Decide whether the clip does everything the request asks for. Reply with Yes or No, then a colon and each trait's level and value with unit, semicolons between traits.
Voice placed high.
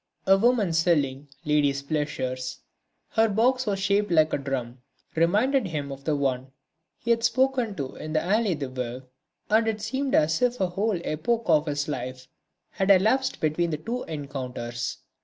No: medium, 165 Hz